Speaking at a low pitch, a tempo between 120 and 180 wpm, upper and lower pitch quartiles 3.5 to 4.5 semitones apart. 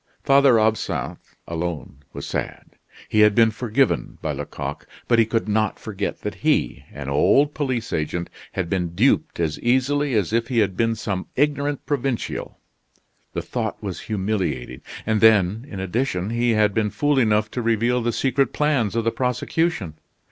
Yes: low, 110 Hz; average, 165 wpm; average, 4.2 semitones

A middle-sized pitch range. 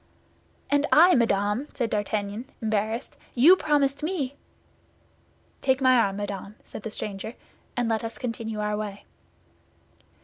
Yes: average, 4.3 semitones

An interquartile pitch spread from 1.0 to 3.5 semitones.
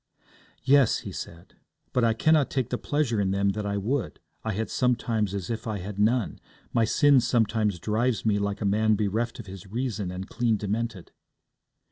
Yes: average, 2.9 semitones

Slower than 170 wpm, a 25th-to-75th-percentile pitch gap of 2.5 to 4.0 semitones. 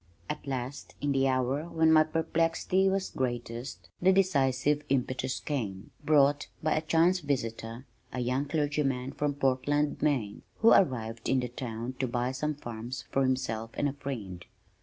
Yes: average, 160 wpm; average, 3.4 semitones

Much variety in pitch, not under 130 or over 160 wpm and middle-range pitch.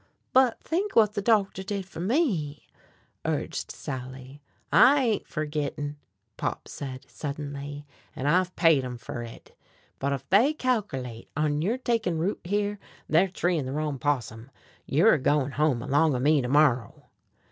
Yes: wide, 6.4 semitones; average, 155 wpm; medium, 150 Hz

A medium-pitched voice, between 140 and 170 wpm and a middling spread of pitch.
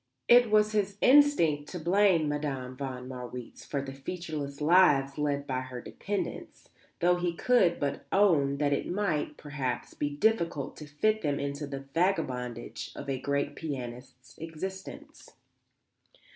Yes: medium, 150 Hz; average, 145 wpm; average, 4.8 semitones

